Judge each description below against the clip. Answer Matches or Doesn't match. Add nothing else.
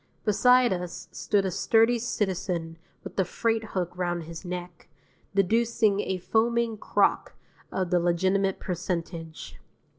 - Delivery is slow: Matches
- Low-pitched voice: Doesn't match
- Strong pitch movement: Doesn't match